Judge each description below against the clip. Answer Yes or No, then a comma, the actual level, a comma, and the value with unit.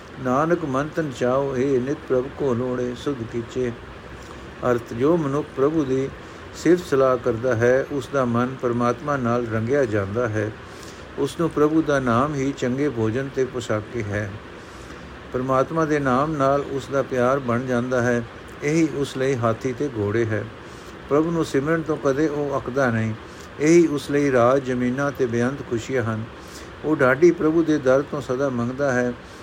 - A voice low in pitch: Yes, low, 130 Hz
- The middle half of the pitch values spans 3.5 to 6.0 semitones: No, average, 2.9 semitones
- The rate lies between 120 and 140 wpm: No, fast, 165 wpm